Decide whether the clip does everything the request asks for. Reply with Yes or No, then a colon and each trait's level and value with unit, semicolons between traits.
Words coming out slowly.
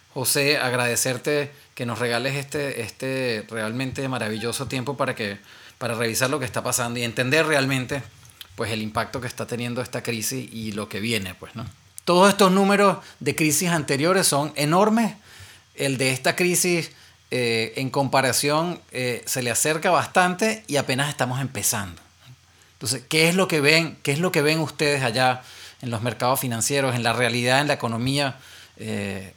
No: average, 170 wpm